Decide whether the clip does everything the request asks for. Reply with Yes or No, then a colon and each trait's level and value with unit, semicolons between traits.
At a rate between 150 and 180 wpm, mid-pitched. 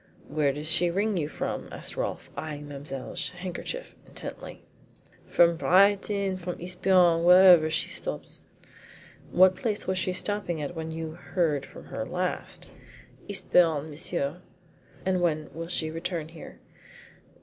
No: average, 140 wpm; medium, 170 Hz